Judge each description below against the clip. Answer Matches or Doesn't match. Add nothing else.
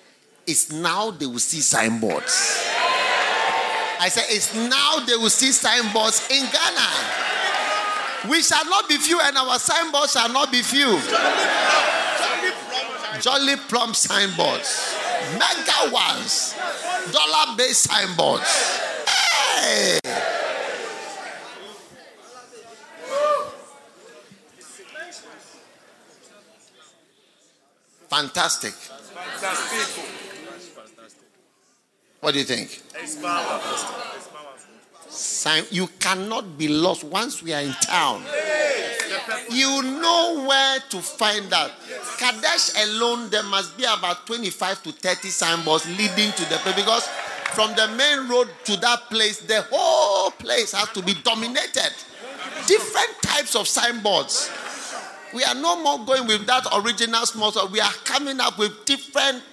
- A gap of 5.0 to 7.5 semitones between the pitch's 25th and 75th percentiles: Matches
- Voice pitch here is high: Matches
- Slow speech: Matches